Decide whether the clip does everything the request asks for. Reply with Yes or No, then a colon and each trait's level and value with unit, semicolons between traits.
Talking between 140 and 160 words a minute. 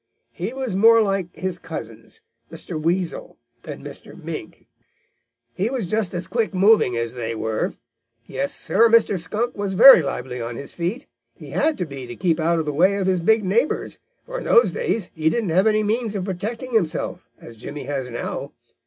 No: average, 190 wpm